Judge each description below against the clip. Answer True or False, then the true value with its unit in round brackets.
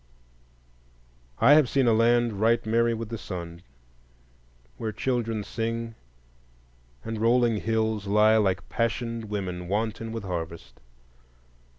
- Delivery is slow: True (115 wpm)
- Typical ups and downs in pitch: False (2.1 semitones)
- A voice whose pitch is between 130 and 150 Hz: False (110 Hz)